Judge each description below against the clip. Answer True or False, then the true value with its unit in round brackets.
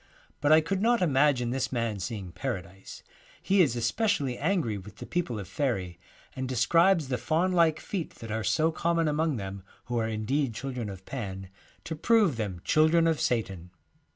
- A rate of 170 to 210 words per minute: True (180 wpm)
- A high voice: False (130 Hz)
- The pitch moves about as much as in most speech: False (7.1 semitones)